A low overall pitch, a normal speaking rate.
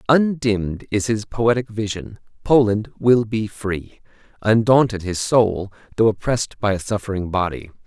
No: low, 110 Hz; slow, 120 wpm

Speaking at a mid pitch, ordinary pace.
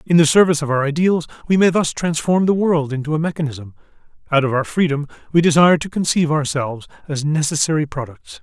Yes: medium, 155 Hz; average, 190 wpm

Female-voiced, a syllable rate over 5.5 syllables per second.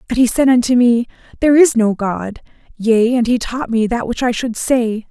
No: female; 5.0 syllables/s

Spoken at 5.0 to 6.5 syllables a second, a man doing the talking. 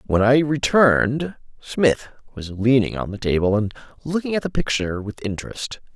Yes: 5.2 syllables/s; male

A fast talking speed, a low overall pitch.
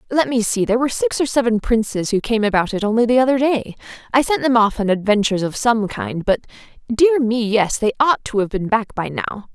No: fast, 235 wpm; high, 225 Hz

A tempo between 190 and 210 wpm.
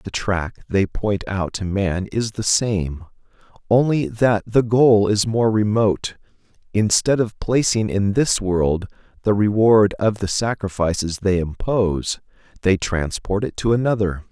No: average, 145 wpm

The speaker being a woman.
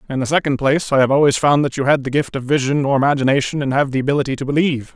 No: male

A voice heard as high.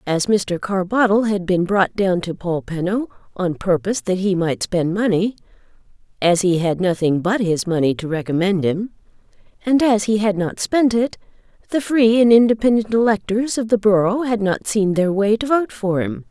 Yes: high, 200 Hz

